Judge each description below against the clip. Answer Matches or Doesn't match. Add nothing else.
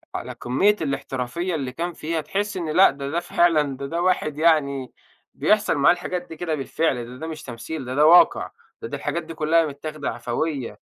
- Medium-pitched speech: Matches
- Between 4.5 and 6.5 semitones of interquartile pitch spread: Doesn't match